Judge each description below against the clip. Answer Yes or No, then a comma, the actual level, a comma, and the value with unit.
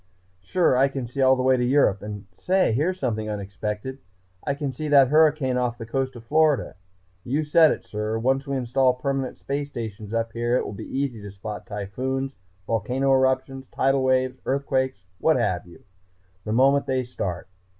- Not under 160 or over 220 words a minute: Yes, average, 185 wpm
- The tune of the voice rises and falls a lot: No, average, 3.4 semitones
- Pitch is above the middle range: No, low, 130 Hz